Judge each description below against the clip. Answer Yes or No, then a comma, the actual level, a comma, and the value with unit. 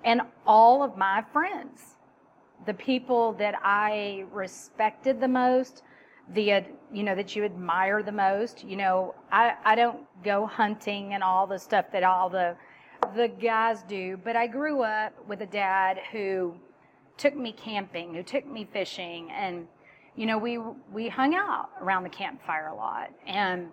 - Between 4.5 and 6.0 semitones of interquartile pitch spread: No, average, 3.5 semitones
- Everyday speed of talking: Yes, average, 165 wpm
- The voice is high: Yes, high, 210 Hz